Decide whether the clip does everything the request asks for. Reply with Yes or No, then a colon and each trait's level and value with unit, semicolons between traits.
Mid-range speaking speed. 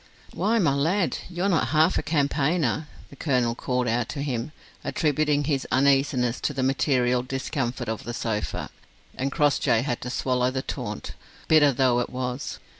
Yes: average, 165 wpm